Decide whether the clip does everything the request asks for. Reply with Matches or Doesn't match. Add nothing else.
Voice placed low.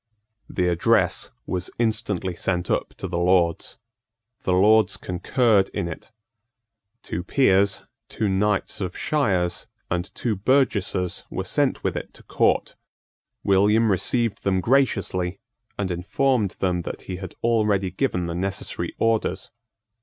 Matches